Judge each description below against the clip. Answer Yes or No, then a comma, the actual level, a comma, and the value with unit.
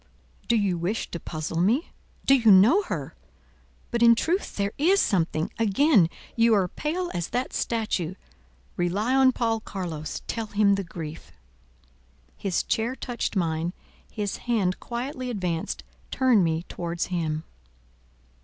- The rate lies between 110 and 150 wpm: Yes, average, 140 wpm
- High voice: Yes, high, 205 Hz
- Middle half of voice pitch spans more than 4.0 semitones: Yes, wide, 5.6 semitones